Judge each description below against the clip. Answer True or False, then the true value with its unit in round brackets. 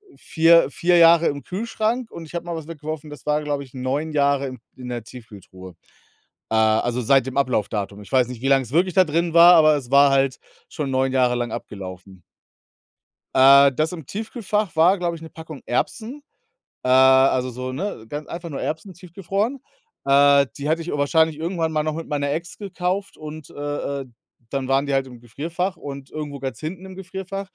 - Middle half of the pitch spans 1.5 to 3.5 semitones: False (4.4 semitones)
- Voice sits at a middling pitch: True (145 Hz)